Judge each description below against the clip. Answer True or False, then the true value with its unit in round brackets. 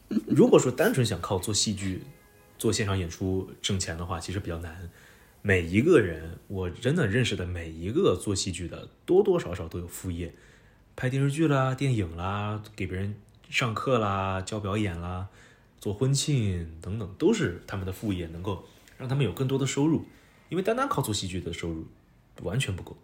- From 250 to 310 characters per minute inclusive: True (275 characters per minute)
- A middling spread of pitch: True (4.3 semitones)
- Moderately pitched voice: False (100 Hz)